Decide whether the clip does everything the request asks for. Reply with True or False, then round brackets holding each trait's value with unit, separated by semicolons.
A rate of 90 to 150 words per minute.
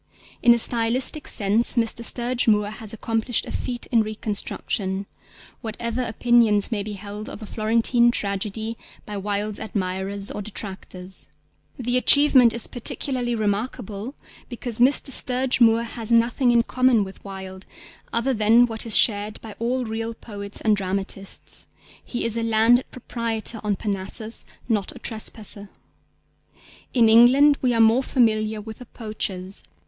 True (145 wpm)